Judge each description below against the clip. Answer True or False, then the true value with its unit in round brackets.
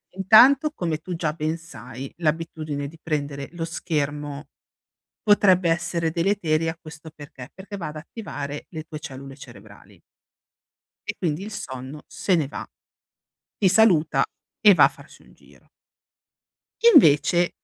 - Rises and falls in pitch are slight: False (3.5 semitones)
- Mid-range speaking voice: True (160 Hz)